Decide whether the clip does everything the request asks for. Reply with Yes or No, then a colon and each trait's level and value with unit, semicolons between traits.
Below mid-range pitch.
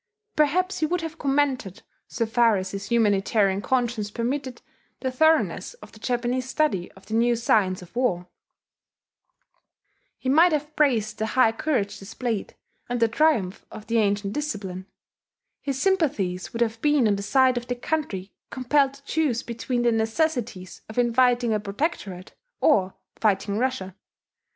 No: high, 235 Hz